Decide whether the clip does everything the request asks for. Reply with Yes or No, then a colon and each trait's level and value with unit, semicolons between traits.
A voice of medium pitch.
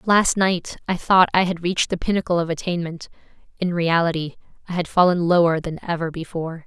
Yes: medium, 170 Hz